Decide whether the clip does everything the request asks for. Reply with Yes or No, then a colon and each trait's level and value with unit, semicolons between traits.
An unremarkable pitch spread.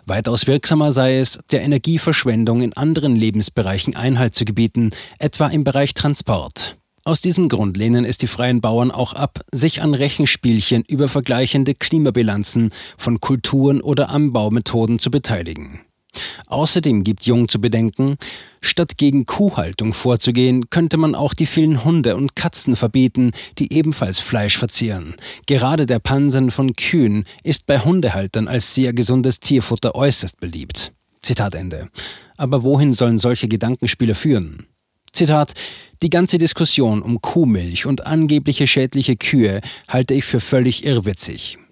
Yes: average, 4.0 semitones